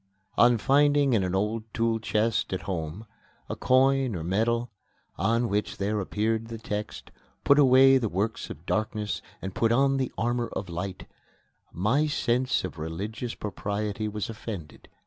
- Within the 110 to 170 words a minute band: Yes, average, 155 wpm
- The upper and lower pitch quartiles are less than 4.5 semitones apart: Yes, average, 3.3 semitones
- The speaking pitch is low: Yes, low, 110 Hz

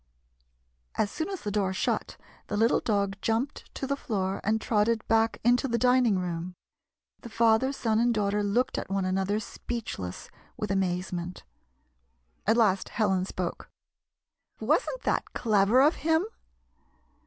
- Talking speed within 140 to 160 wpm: Yes, average, 150 wpm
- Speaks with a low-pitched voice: No, high, 215 Hz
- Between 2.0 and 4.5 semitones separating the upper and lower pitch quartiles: Yes, average, 3.7 semitones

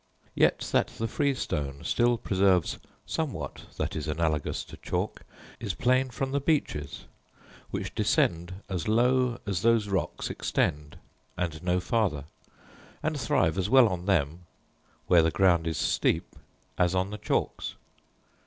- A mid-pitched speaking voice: No, very low, 95 Hz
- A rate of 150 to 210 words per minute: No, average, 140 wpm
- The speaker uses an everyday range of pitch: No, wide, 6.1 semitones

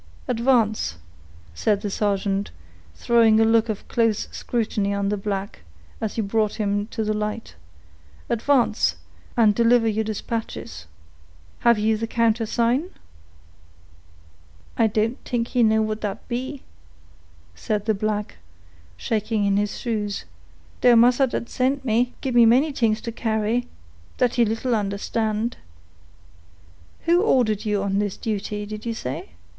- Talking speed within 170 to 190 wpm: No, average, 140 wpm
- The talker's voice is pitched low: No, high, 220 Hz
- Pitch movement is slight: Yes, narrow, 2.2 semitones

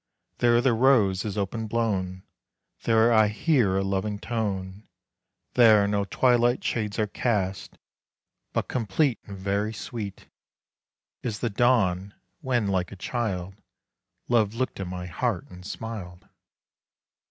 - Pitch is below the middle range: Yes, low, 105 Hz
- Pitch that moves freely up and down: No, average, 3.5 semitones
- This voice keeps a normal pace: No, slow, 130 wpm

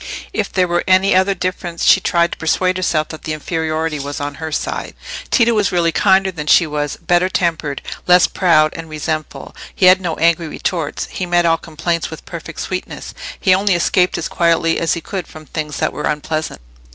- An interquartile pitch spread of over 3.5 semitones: No, average, 2.8 semitones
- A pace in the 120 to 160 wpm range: No, average, 200 wpm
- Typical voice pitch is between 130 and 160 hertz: No, medium, 170 Hz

